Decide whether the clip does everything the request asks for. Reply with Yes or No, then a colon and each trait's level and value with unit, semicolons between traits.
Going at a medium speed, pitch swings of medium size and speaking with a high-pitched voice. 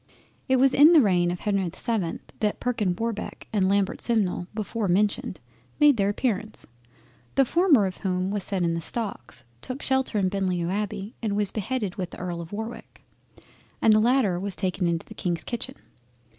Yes: average, 185 wpm; average, 4.0 semitones; high, 205 Hz